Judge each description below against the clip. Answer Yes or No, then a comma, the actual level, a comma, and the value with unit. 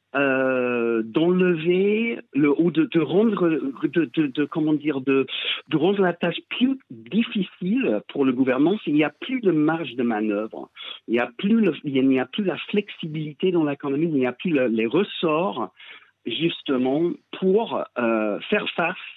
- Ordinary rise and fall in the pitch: No, wide, 7.5 semitones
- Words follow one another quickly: No, average, 175 wpm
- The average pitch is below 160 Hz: No, medium, 165 Hz